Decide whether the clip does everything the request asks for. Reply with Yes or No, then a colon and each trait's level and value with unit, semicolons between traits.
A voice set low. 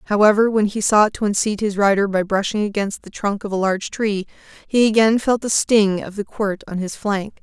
No: high, 205 Hz